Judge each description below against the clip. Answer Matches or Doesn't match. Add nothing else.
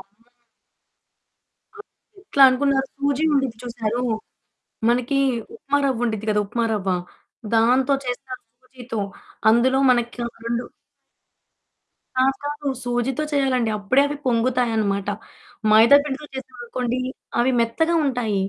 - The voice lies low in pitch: Doesn't match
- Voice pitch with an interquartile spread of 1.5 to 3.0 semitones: Matches